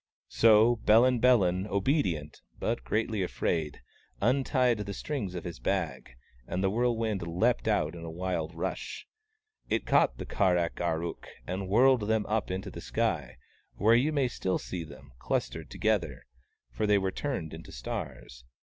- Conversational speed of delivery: Yes, average, 165 wpm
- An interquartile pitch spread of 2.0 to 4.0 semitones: No, average, 5.2 semitones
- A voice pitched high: No, low, 100 Hz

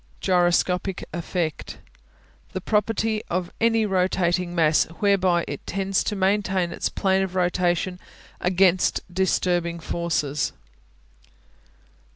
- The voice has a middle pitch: Yes, medium, 180 Hz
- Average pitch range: No, narrow, 1.8 semitones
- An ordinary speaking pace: No, slow, 100 wpm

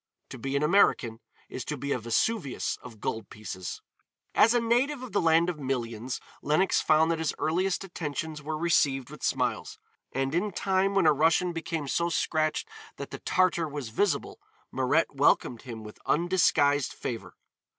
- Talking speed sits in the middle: Yes, average, 170 wpm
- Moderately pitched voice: Yes, medium, 155 Hz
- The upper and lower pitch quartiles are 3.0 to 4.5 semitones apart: No, average, 5.0 semitones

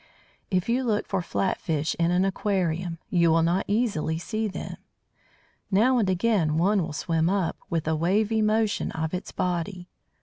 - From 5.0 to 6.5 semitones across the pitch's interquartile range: No, average, 4.0 semitones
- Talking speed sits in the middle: Yes, average, 170 wpm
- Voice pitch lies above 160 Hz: Yes, medium, 185 Hz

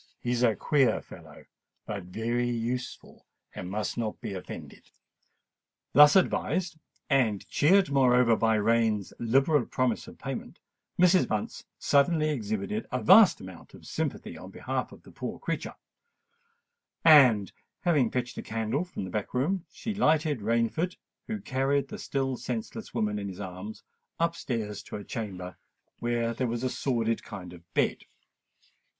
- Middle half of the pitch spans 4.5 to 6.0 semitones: Yes, average, 5.3 semitones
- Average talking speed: Yes, average, 150 wpm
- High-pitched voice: No, low, 120 Hz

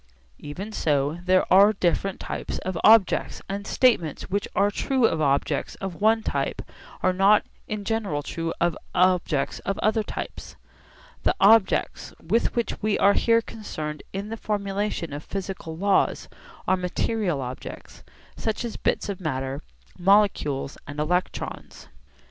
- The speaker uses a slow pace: No, average, 145 wpm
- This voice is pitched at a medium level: No, high, 195 Hz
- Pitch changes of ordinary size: Yes, average, 4.6 semitones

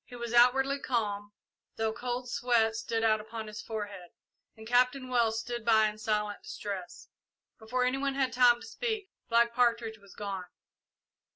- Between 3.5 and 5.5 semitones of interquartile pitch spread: No, narrow, 2.5 semitones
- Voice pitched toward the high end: Yes, high, 230 Hz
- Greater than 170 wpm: No, average, 165 wpm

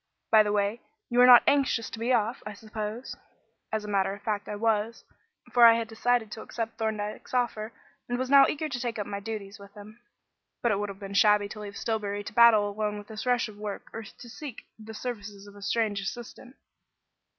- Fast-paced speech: Yes, fast, 220 wpm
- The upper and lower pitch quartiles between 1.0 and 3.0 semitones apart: Yes, narrow, 2.4 semitones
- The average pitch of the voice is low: No, high, 215 Hz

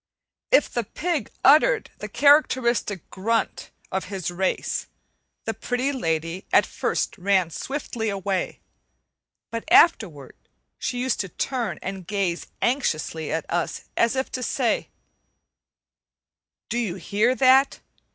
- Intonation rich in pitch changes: Yes, wide, 5.8 semitones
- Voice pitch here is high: Yes, high, 220 Hz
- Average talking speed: No, slow, 120 wpm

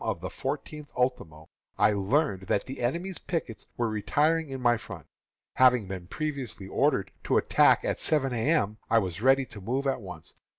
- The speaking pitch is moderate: No, low, 125 Hz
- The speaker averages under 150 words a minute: No, average, 180 wpm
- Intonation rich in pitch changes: Yes, wide, 5.8 semitones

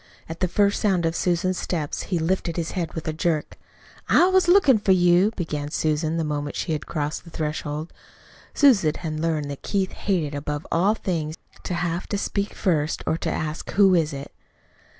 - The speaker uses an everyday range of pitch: Yes, average, 3.4 semitones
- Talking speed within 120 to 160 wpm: No, average, 190 wpm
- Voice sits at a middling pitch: Yes, medium, 165 Hz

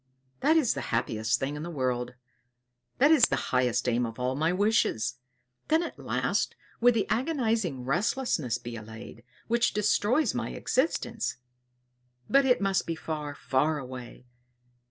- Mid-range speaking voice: Yes, medium, 155 Hz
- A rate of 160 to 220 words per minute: No, average, 150 wpm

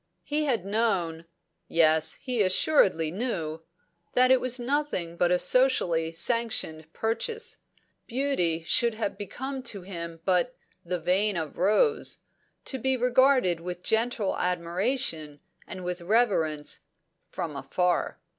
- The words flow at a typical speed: No, slow, 125 wpm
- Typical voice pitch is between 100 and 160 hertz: No, high, 190 Hz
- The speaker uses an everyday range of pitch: No, wide, 6.9 semitones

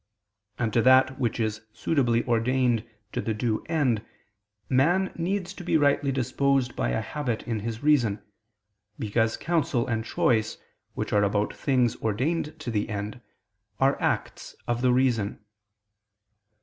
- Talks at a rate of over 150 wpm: No, average, 145 wpm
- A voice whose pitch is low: Yes, low, 120 Hz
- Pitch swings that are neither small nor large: Yes, average, 3.8 semitones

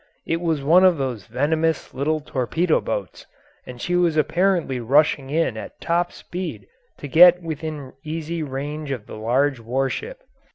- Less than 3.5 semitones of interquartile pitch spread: No, average, 3.9 semitones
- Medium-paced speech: Yes, average, 155 wpm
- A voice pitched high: No, medium, 155 Hz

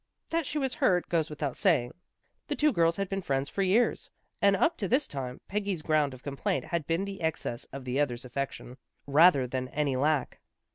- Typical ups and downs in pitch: No, wide, 6.3 semitones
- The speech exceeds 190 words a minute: Yes, average, 200 wpm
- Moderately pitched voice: Yes, medium, 155 Hz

